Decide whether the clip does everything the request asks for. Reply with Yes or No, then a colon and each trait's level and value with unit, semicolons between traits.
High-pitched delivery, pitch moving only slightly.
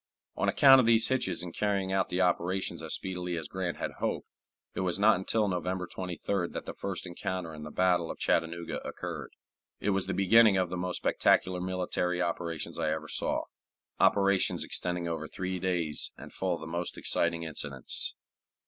No: very low, 90 Hz; narrow, 1.9 semitones